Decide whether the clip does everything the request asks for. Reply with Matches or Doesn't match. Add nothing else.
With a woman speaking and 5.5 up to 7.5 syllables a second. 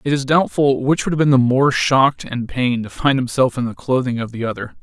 Doesn't match